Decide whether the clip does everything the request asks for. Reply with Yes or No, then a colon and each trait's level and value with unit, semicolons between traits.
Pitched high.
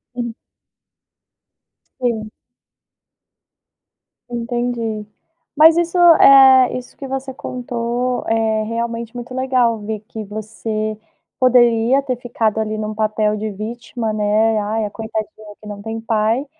Yes: high, 225 Hz